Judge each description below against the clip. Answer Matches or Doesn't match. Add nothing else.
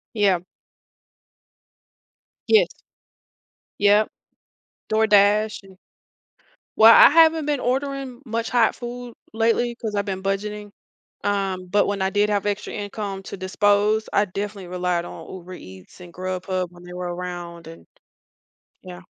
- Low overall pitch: Doesn't match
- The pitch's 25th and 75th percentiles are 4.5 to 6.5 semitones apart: Doesn't match